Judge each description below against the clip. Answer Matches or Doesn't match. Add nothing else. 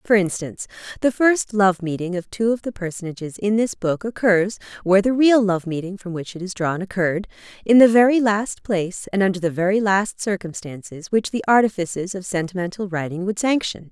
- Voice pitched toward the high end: Matches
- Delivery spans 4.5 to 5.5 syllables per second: Matches